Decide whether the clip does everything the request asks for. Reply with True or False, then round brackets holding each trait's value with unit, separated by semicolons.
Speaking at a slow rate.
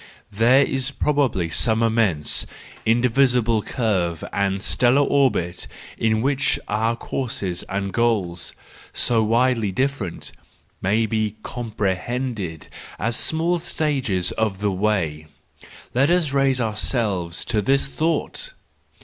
True (105 wpm)